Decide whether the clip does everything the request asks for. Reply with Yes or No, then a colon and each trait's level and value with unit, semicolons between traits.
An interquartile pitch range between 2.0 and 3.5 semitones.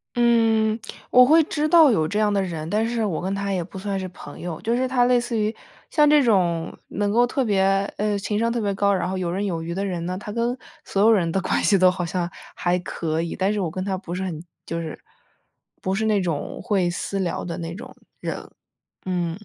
No: average, 4.1 semitones